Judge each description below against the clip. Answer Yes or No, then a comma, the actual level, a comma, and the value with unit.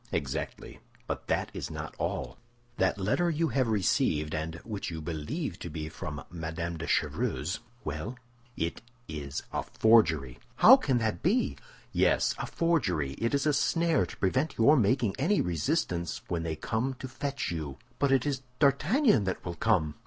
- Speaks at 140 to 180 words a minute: Yes, average, 165 wpm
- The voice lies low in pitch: Yes, low, 105 Hz